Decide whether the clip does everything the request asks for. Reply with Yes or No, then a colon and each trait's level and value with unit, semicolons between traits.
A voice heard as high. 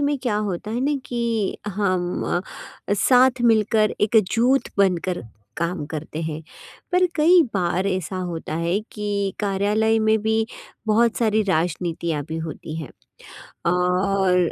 Yes: high, 200 Hz